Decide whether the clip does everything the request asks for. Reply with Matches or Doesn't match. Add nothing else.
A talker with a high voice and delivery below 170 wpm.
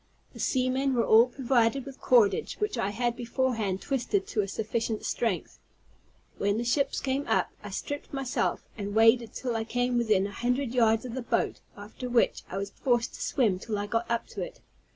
Doesn't match